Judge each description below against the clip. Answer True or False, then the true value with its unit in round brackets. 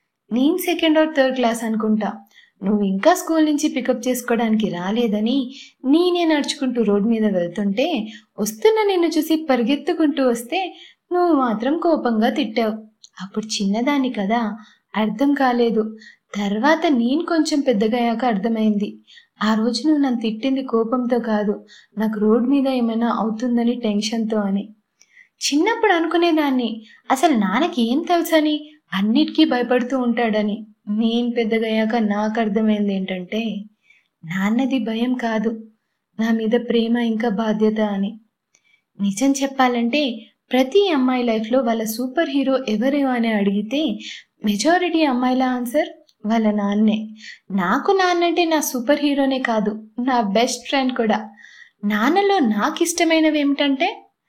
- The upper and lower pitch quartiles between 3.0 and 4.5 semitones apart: False (5.0 semitones)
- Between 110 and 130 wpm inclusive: True (115 wpm)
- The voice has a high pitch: True (240 Hz)